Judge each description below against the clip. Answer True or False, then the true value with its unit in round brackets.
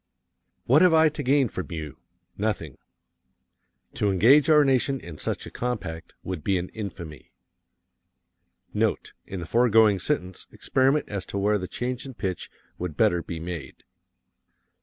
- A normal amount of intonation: False (6.8 semitones)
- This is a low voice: True (100 Hz)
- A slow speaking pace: False (150 wpm)